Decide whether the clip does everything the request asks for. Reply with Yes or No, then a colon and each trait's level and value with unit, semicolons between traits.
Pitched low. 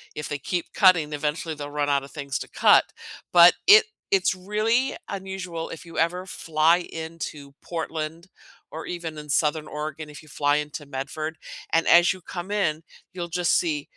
No: medium, 160 Hz